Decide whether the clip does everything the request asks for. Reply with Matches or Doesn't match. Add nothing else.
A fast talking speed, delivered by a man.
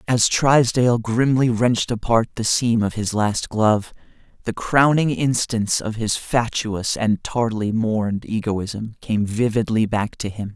Doesn't match